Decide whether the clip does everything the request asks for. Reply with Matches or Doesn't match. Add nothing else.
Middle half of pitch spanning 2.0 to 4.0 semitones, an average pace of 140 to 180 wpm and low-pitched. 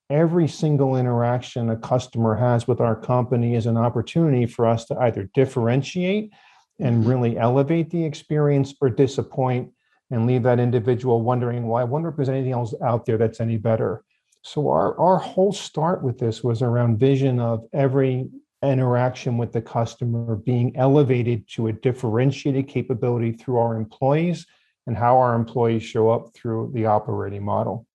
Matches